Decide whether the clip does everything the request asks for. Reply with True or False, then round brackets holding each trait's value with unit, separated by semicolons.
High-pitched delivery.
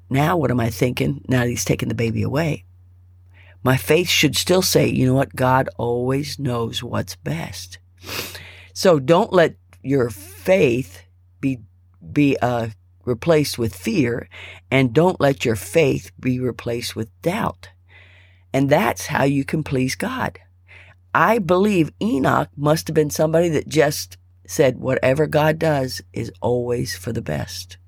False (120 Hz)